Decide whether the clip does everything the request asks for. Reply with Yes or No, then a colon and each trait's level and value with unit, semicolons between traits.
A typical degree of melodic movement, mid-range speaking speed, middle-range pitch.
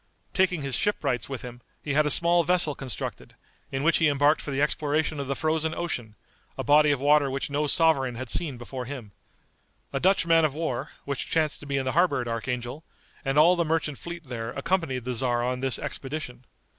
No: average, 3.6 semitones; fast, 210 wpm; medium, 145 Hz